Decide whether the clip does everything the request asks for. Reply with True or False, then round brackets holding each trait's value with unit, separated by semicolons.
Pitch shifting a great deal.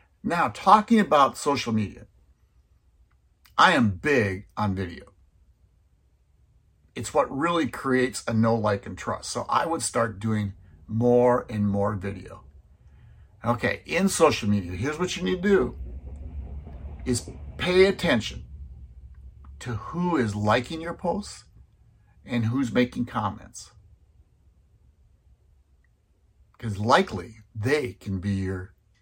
True (6.9 semitones)